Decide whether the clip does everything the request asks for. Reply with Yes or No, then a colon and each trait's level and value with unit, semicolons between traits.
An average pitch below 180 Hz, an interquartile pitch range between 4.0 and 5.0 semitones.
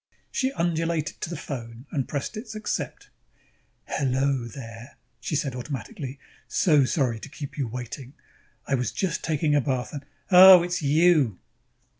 Yes: medium, 140 Hz; average, 4.7 semitones